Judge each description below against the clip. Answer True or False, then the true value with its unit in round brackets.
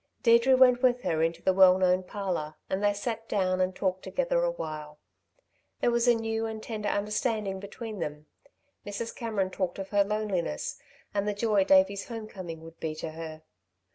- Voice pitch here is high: True (200 Hz)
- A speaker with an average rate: True (180 wpm)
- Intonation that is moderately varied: True (3.5 semitones)